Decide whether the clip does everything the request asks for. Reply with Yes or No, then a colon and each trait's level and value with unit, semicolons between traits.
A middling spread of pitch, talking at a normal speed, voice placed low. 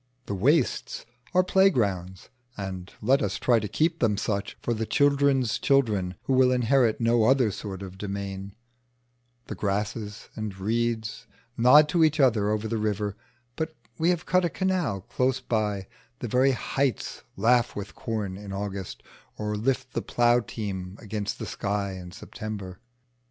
Yes: average, 4.5 semitones; average, 155 wpm; low, 110 Hz